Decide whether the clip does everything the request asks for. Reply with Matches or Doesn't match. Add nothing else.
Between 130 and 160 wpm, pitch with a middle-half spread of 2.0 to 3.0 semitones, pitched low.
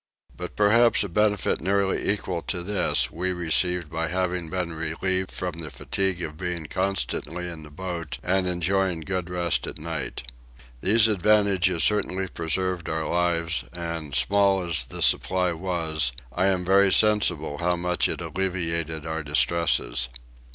Matches